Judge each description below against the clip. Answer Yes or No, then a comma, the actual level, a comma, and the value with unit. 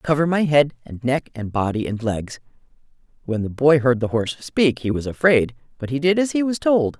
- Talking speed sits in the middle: No, fast, 225 wpm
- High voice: No, low, 135 Hz